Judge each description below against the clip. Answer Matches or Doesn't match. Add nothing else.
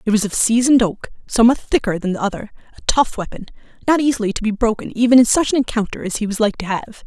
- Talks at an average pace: Doesn't match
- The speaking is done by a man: Doesn't match